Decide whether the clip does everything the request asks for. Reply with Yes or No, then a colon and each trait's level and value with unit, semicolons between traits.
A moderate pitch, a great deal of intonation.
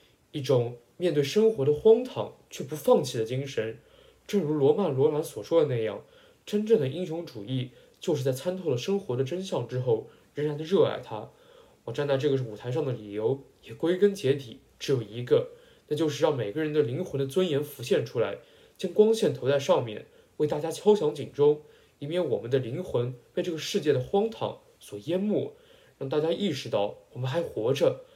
Yes: medium, 150 Hz; wide, 7.3 semitones